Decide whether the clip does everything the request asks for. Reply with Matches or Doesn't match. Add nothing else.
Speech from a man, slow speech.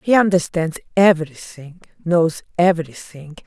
Doesn't match